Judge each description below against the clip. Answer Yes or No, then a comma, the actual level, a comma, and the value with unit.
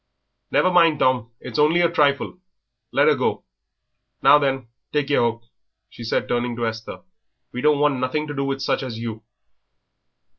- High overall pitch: No, low, 135 Hz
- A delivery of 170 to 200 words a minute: Yes, average, 180 wpm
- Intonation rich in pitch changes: No, average, 3.9 semitones